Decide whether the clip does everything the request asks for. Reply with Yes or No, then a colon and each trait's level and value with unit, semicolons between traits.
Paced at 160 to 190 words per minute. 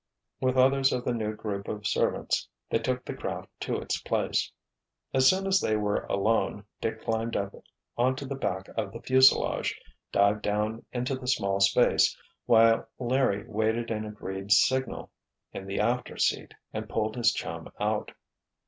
Yes: average, 165 wpm